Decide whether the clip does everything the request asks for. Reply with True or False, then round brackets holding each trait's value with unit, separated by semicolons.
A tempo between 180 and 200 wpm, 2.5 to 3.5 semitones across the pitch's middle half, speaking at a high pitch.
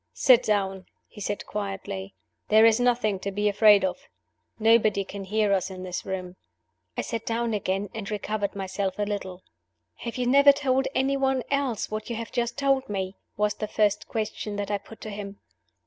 True (185 wpm; 2.8 semitones; 210 Hz)